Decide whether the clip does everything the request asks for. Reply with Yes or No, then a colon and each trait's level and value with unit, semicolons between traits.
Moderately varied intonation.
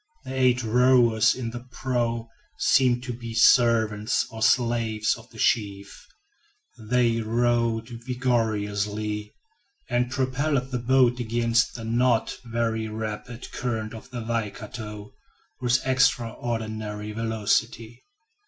No: narrow, 1.9 semitones